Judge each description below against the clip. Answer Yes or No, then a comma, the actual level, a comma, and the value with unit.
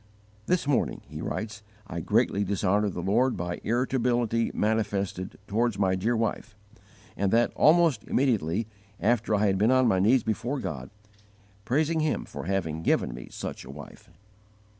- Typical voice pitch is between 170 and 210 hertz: No, low, 110 Hz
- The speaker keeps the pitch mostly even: No, average, 4.1 semitones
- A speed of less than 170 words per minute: Yes, average, 155 wpm